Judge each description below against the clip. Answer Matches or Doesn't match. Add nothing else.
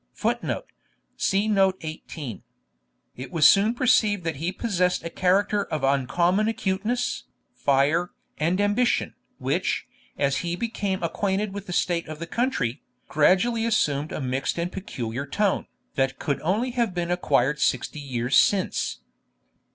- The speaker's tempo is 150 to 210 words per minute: Doesn't match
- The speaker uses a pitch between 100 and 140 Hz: Doesn't match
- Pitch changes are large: Matches